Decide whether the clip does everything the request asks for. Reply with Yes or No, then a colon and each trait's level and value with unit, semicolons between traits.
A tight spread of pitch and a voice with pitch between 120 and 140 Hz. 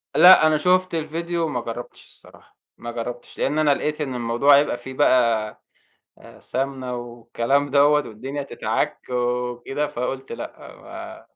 No: average, 3.5 semitones; low, 135 Hz